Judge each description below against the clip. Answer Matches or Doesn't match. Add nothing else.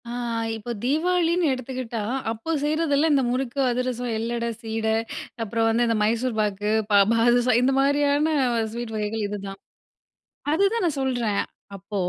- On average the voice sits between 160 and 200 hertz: Doesn't match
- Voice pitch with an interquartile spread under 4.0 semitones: Doesn't match